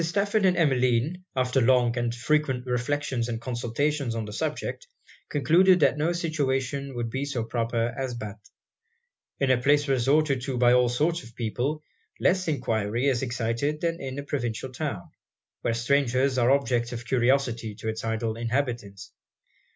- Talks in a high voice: No, low, 130 Hz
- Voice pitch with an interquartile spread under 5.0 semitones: Yes, average, 3.4 semitones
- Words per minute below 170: Yes, average, 160 wpm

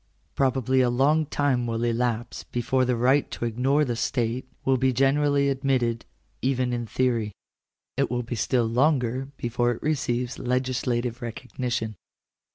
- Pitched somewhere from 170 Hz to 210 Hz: No, low, 125 Hz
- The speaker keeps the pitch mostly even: Yes, narrow, 1.9 semitones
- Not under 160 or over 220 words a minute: No, average, 150 wpm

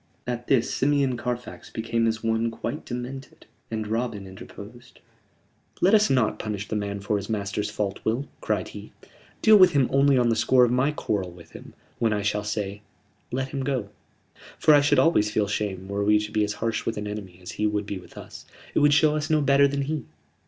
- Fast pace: Yes, fast, 215 wpm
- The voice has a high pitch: No, low, 115 Hz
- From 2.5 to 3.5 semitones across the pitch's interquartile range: No, average, 4.7 semitones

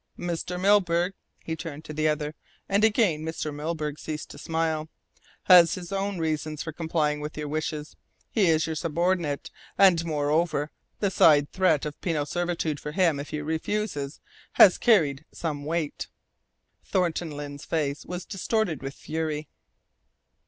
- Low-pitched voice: No, medium, 160 Hz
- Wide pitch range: No, average, 2.8 semitones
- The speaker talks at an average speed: Yes, average, 150 wpm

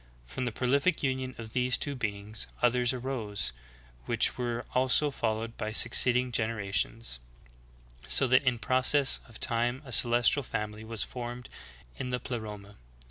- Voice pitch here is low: Yes, low, 120 Hz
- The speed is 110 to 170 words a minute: Yes, average, 150 wpm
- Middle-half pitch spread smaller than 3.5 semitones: Yes, average, 2.7 semitones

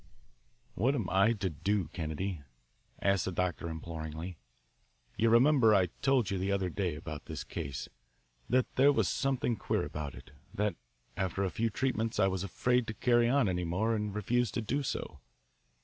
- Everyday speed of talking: Yes, average, 175 wpm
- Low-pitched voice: Yes, low, 100 Hz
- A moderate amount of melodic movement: Yes, average, 5.0 semitones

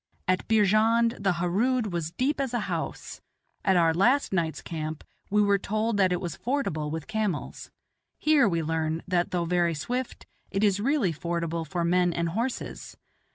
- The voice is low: No, medium, 185 Hz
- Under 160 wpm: No, average, 170 wpm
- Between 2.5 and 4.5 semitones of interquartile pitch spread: No, average, 4.9 semitones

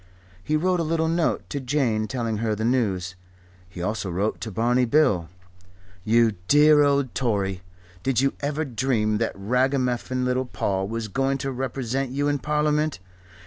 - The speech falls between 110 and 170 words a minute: Yes, average, 160 wpm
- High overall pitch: No, low, 125 Hz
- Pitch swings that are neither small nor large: Yes, average, 4.6 semitones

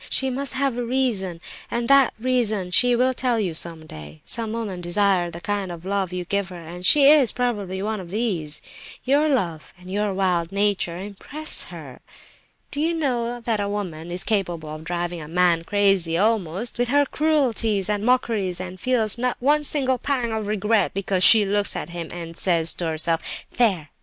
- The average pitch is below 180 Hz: No, high, 200 Hz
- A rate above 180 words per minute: Yes, average, 190 wpm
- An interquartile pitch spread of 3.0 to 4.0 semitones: No, wide, 5.5 semitones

